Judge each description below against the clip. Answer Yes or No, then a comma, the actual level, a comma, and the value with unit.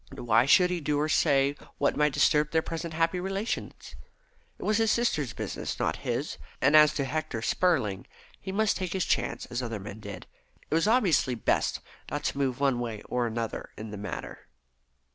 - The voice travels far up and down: Yes, wide, 6.4 semitones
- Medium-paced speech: Yes, average, 195 wpm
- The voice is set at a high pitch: No, medium, 145 Hz